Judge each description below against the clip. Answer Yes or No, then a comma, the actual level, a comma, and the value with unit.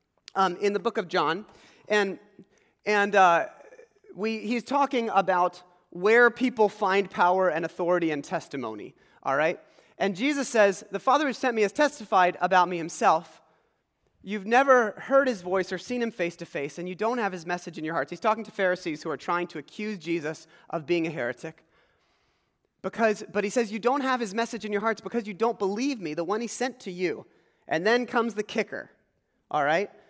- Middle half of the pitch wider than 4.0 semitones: Yes, average, 4.8 semitones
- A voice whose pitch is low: No, high, 205 Hz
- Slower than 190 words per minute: No, average, 200 wpm